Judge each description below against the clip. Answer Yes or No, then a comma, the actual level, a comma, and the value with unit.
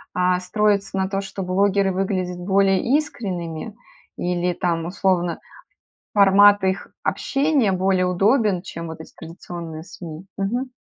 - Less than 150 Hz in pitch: No, high, 190 Hz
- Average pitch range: No, narrow, 2.2 semitones